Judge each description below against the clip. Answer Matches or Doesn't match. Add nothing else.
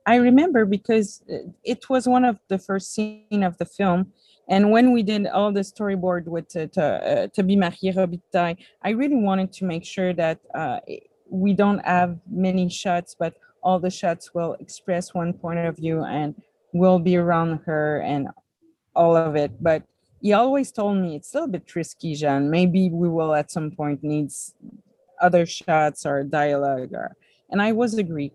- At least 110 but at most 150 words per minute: Doesn't match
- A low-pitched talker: Doesn't match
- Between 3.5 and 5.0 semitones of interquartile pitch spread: Matches